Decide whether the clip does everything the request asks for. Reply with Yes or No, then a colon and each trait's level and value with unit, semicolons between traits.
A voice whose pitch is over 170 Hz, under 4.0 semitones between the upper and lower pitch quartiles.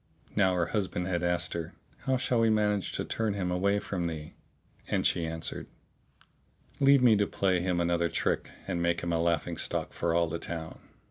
No: very low, 90 Hz; average, 3.2 semitones